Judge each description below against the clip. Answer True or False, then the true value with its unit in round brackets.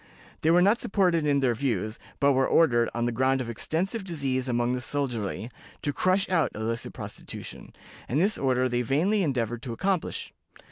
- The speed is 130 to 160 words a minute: False (185 wpm)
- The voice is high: False (135 Hz)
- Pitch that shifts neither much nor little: False (5.7 semitones)